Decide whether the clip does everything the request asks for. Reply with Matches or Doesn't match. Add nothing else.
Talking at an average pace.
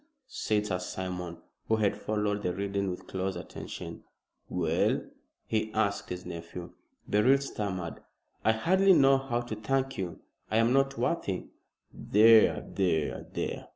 Matches